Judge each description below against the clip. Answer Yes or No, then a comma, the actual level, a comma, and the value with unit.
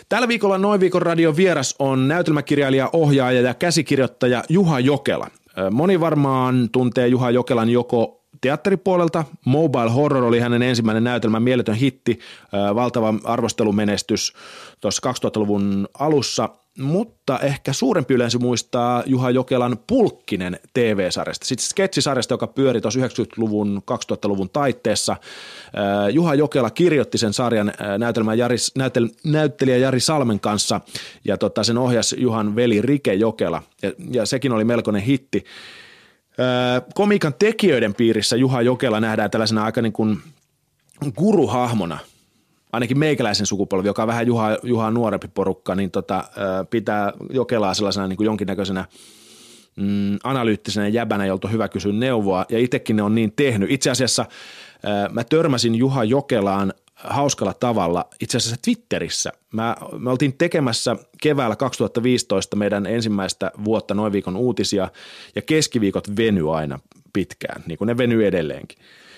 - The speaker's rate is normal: Yes, average, 130 wpm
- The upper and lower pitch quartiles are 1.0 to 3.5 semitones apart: No, average, 4.4 semitones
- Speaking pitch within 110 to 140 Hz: Yes, low, 120 Hz